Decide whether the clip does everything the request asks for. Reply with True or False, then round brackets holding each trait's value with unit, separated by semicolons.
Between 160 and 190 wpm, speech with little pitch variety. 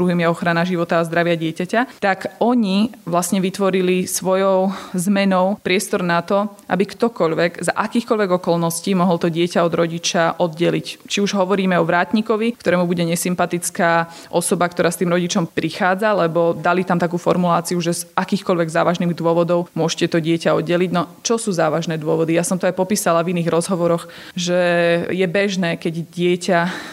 True (165 wpm; 2.1 semitones)